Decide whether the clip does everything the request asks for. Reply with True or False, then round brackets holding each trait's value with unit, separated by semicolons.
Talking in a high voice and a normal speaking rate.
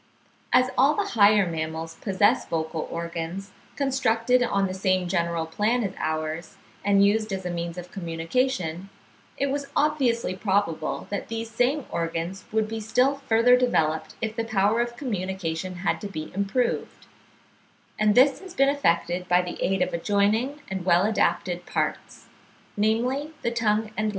True (200 Hz; 160 wpm)